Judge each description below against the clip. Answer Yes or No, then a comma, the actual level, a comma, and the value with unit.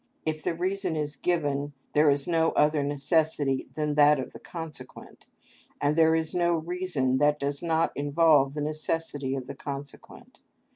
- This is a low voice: No, medium, 150 Hz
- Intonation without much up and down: Yes, narrow, 2.3 semitones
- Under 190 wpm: Yes, average, 160 wpm